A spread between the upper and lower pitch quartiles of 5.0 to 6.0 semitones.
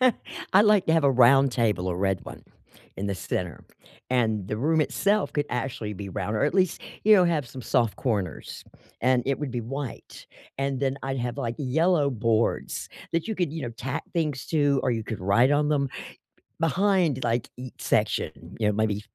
Yes: average, 5.3 semitones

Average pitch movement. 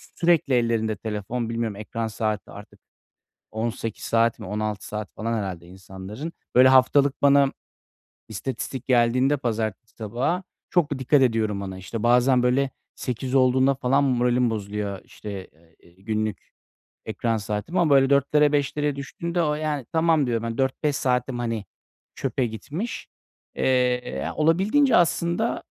Yes: average, 4.5 semitones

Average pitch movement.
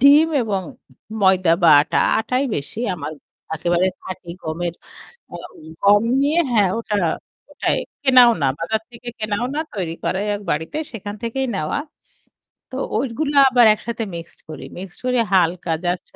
No: wide, 5.8 semitones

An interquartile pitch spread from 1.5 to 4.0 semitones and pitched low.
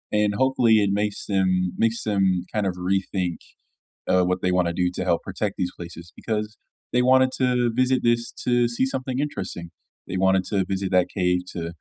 No: average, 4.5 semitones; very low, 95 Hz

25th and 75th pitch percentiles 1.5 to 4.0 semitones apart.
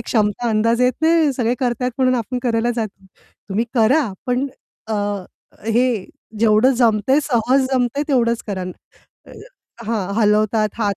Yes: average, 2.9 semitones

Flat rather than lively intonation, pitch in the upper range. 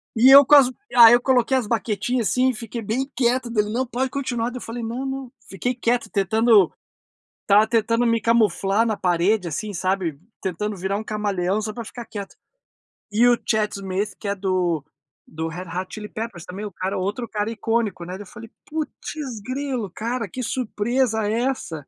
No: average, 3.5 semitones; high, 220 Hz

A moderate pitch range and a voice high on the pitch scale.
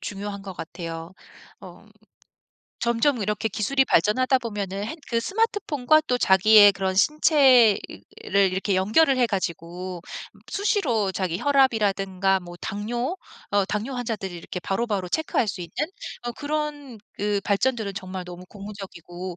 Yes: average, 4.9 semitones; high, 205 Hz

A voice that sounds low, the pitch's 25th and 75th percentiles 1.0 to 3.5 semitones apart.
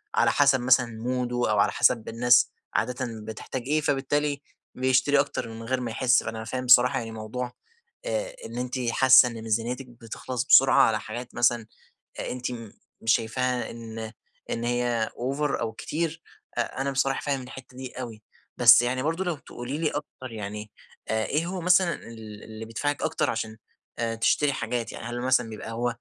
Yes: low, 125 Hz; average, 2.9 semitones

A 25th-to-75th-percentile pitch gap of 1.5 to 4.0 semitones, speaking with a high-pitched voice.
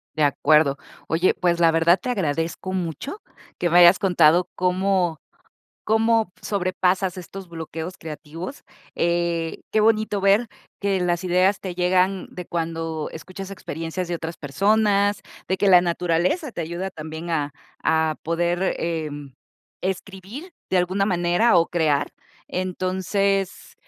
No: average, 2.8 semitones; medium, 180 Hz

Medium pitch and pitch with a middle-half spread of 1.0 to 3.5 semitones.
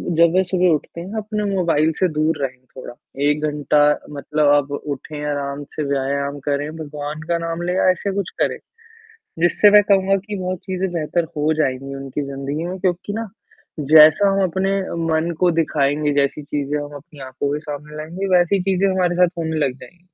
No: medium, 155 Hz; average, 4.1 semitones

